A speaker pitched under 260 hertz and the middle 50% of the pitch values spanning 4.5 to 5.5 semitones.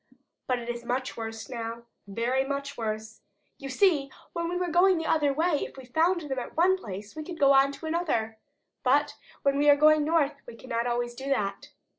No: very high, 275 Hz; average, 4.8 semitones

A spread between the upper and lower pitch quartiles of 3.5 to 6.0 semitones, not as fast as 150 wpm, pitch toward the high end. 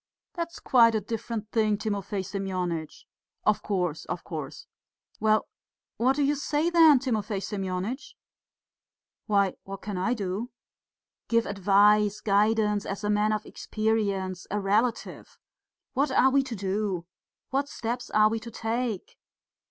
No: average, 3.0 semitones; slow, 135 wpm; high, 210 Hz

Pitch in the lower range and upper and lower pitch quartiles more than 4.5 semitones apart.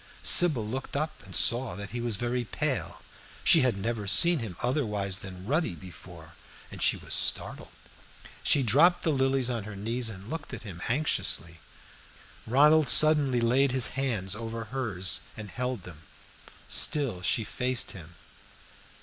Yes: low, 120 Hz; average, 5.2 semitones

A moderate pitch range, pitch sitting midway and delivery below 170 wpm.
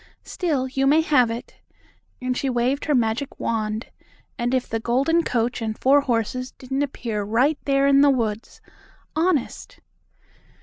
No: average, 3.3 semitones; very high, 255 Hz; average, 155 wpm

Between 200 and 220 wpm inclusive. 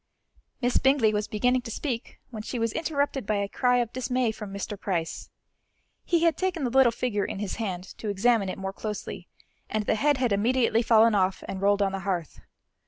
Yes: fast, 205 wpm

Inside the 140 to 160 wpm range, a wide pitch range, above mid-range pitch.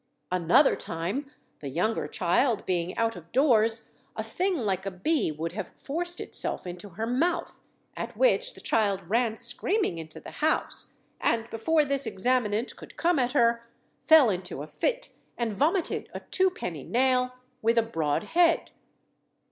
Yes: average, 155 wpm; wide, 7.7 semitones; high, 230 Hz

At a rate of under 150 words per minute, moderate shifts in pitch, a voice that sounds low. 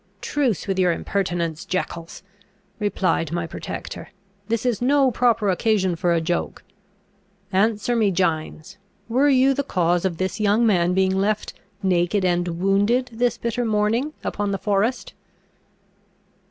No: average, 140 wpm; average, 4.6 semitones; high, 200 Hz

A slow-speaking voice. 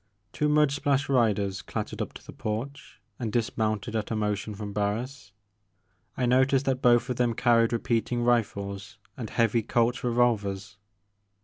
No: average, 150 wpm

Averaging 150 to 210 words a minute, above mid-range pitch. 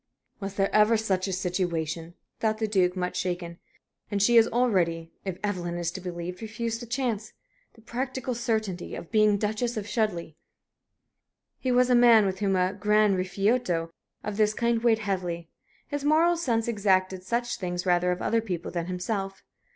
Yes: average, 175 wpm; high, 200 Hz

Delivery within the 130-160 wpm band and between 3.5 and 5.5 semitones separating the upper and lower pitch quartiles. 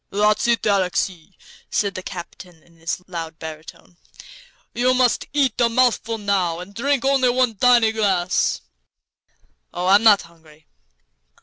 Yes: average, 140 wpm; average, 5.2 semitones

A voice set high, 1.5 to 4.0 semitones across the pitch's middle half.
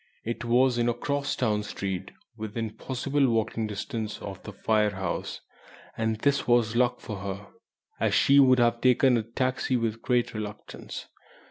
No: low, 115 Hz; average, 3.0 semitones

